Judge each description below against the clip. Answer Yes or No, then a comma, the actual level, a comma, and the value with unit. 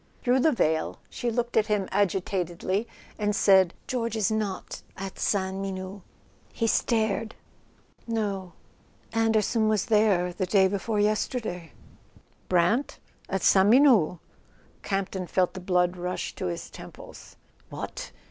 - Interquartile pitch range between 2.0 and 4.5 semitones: Yes, average, 2.9 semitones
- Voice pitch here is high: Yes, high, 200 Hz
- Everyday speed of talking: No, slow, 130 wpm